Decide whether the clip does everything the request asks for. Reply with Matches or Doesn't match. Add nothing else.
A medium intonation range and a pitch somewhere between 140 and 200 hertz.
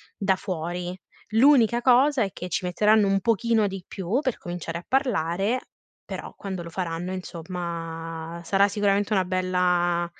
Matches